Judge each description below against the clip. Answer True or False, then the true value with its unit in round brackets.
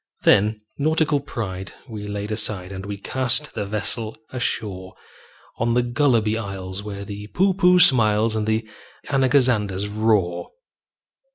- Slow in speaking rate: True (125 wpm)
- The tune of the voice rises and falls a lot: False (3.6 semitones)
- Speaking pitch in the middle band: False (110 Hz)